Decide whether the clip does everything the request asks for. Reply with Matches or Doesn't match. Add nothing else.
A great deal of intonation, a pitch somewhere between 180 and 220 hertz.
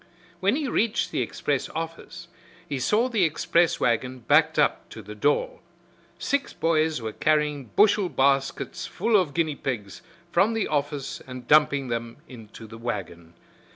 Doesn't match